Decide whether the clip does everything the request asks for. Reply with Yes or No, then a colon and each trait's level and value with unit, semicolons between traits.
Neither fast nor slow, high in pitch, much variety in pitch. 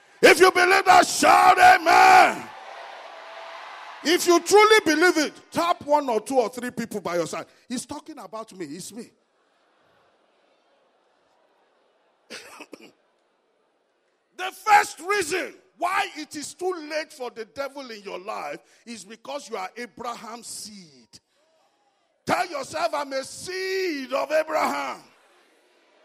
No: slow, 125 wpm; very high, 300 Hz; wide, 7.7 semitones